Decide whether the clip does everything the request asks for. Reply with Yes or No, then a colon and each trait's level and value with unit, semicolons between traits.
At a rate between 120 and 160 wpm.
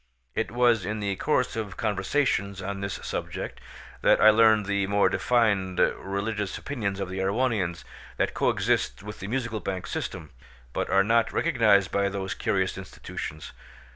Yes: average, 155 wpm